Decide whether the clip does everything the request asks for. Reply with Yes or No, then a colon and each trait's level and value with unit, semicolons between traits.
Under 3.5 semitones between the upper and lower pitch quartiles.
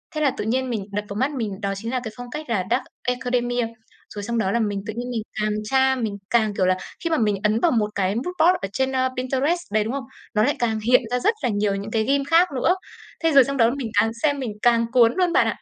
No: average, 3.8 semitones